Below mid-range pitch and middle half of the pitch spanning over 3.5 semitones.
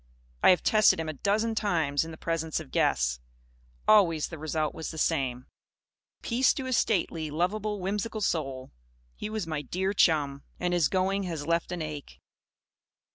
No: medium, 165 Hz; average, 4.7 semitones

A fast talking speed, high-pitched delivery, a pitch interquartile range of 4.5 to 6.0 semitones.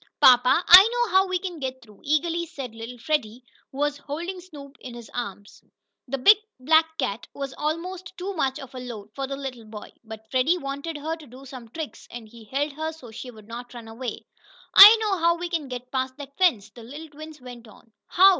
Yes: fast, 215 wpm; very high, 275 Hz; average, 5.0 semitones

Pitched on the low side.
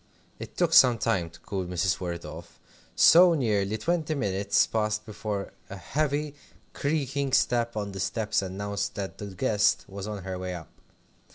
Yes: low, 105 Hz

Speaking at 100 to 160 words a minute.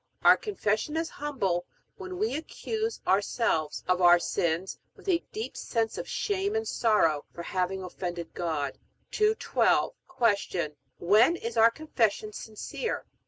Yes: average, 140 wpm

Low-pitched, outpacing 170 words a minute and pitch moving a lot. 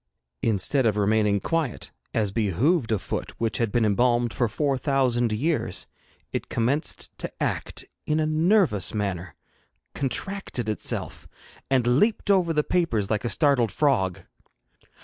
No: low, 120 Hz; average, 140 wpm; wide, 5.9 semitones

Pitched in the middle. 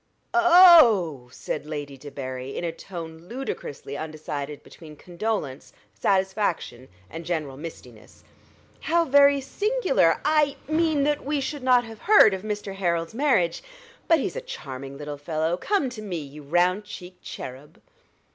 Yes: medium, 180 Hz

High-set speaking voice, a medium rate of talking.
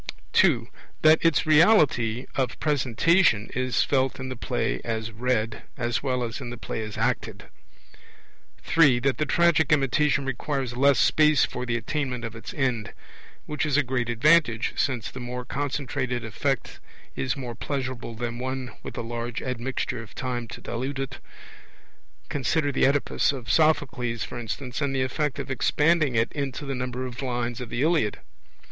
No: low, 130 Hz; average, 165 wpm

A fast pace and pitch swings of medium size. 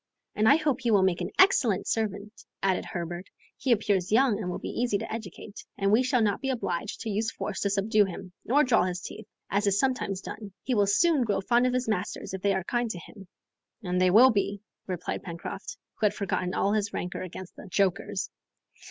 Yes: fast, 220 wpm; average, 3.5 semitones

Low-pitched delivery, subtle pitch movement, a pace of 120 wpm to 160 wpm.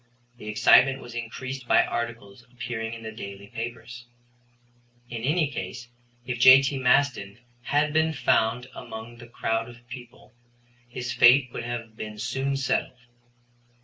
Yes: low, 120 Hz; narrow, 2.3 semitones; average, 140 wpm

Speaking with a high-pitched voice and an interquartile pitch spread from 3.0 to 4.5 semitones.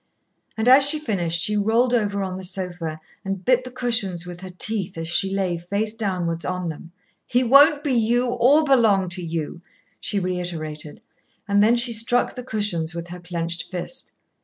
No: high, 195 Hz; wide, 5.4 semitones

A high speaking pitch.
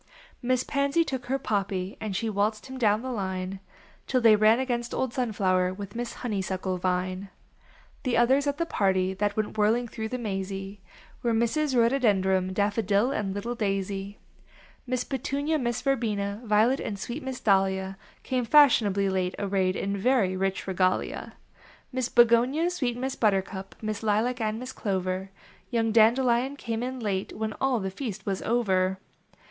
Yes: high, 215 Hz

